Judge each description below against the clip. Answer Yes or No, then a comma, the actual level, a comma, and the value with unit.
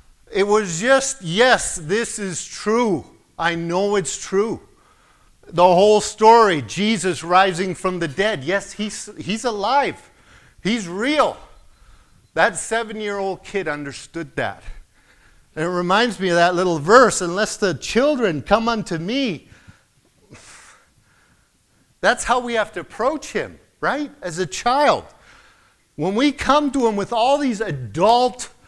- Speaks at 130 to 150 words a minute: Yes, average, 140 wpm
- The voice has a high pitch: Yes, high, 200 Hz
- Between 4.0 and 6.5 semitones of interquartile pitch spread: Yes, average, 4.7 semitones